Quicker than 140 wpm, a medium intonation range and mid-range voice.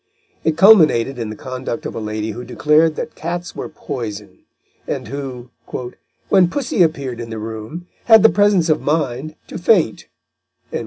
No: average, 160 wpm; wide, 6.6 semitones; medium, 145 Hz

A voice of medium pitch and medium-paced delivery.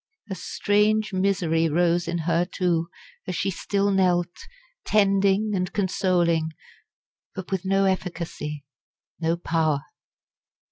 No: medium, 180 Hz; slow, 110 wpm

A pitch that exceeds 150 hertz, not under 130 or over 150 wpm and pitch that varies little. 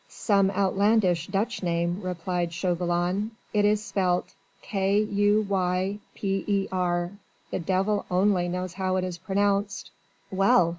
Yes: high, 190 Hz; slow, 135 wpm; narrow, 2.1 semitones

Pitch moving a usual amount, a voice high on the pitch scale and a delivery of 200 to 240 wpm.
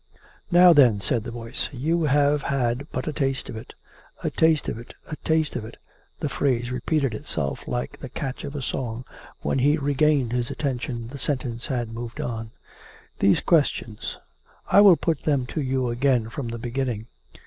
No: average, 3.7 semitones; low, 130 Hz; fast, 205 wpm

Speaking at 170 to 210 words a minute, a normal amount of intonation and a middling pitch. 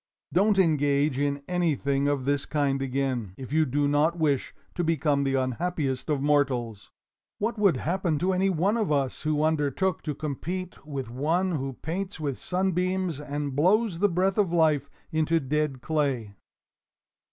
No: average, 160 wpm; average, 4.3 semitones; medium, 150 Hz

